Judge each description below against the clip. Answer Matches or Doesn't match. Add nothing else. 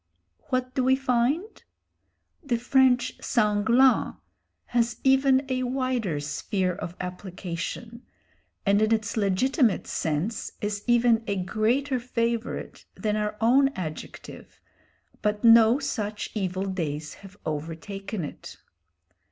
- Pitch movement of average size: Matches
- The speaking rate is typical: Doesn't match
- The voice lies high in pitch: Matches